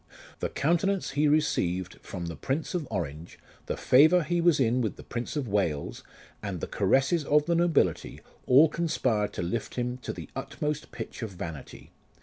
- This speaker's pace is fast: No, average, 175 wpm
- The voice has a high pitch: No, low, 130 Hz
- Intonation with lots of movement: Yes, wide, 7.9 semitones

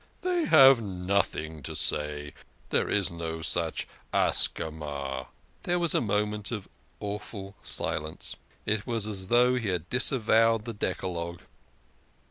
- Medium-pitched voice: No, low, 100 Hz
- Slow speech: Yes, slow, 125 wpm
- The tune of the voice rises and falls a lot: Yes, wide, 5.7 semitones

